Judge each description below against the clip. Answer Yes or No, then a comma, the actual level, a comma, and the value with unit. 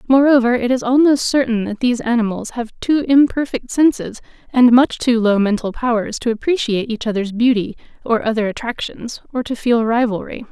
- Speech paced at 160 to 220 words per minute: Yes, average, 170 wpm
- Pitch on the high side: Yes, high, 240 Hz